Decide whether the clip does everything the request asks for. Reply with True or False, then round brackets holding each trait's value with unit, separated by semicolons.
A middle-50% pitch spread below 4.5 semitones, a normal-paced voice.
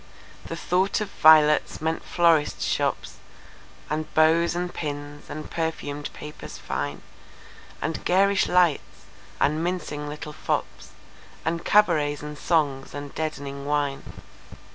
False (2.5 semitones; 105 wpm)